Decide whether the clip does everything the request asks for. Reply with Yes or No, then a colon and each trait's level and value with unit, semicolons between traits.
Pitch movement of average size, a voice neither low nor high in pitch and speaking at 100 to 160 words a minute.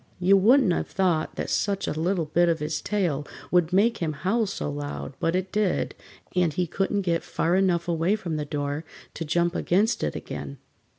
No: average, 3.6 semitones; medium, 175 Hz; average, 195 wpm